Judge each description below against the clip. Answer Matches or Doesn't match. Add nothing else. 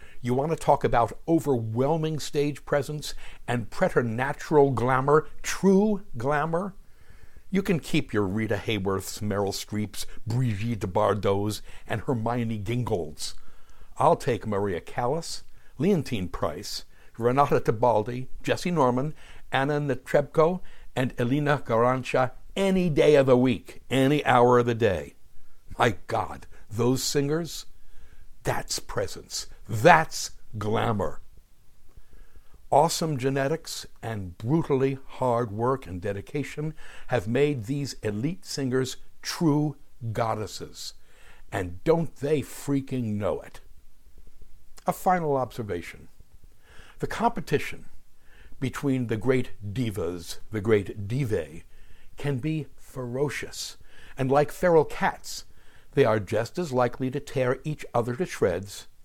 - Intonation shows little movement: Doesn't match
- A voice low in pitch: Matches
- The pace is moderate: Doesn't match